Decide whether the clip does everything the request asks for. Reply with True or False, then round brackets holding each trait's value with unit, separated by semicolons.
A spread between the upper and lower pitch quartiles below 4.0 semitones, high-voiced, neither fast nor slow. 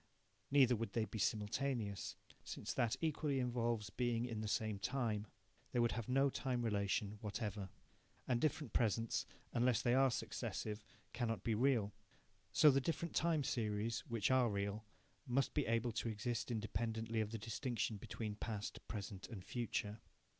False (2.9 semitones; 115 Hz; 155 wpm)